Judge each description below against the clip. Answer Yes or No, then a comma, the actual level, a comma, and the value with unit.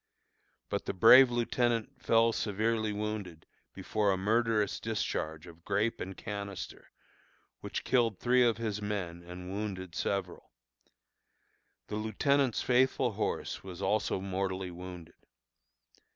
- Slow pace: Yes, slow, 120 wpm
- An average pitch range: Yes, average, 3.6 semitones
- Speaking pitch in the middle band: No, low, 105 Hz